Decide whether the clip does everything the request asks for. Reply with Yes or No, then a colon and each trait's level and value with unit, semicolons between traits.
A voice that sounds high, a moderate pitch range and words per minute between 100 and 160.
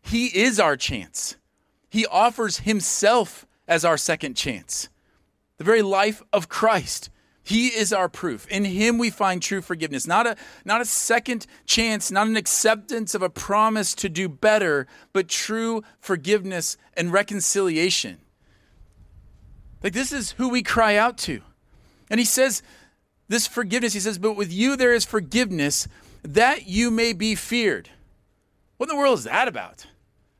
Yes: high, 215 Hz; average, 3.9 semitones; average, 155 wpm